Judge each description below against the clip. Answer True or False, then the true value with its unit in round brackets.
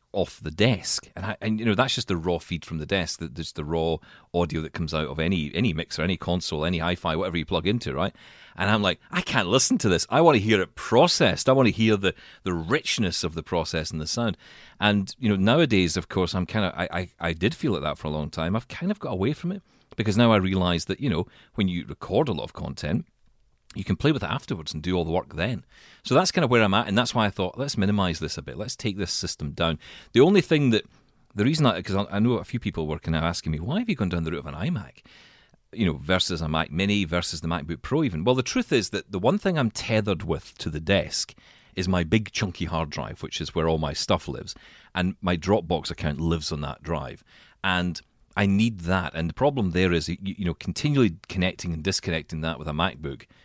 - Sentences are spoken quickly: True (260 wpm)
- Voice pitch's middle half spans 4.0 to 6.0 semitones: True (4.7 semitones)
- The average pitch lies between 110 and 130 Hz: False (90 Hz)